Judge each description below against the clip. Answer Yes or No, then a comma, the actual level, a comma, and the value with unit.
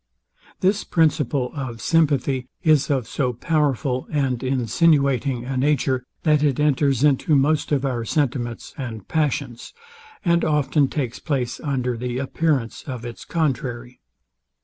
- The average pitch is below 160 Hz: Yes, low, 135 Hz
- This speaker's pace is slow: Yes, slow, 130 wpm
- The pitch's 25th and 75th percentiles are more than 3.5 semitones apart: No, average, 3.1 semitones